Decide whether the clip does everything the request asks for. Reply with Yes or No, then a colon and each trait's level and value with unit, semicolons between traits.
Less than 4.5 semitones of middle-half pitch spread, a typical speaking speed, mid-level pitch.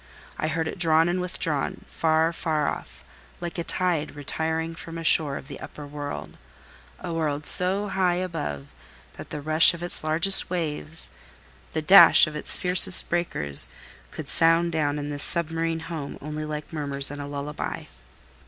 Yes: narrow, 2.5 semitones; average, 160 wpm; medium, 160 Hz